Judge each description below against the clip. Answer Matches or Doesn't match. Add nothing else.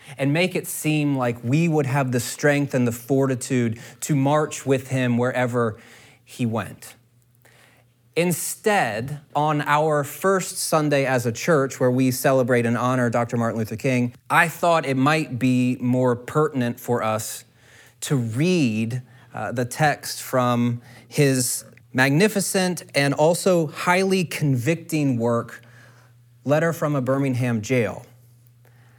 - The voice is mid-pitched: Doesn't match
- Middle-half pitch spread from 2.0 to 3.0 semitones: Doesn't match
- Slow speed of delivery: Matches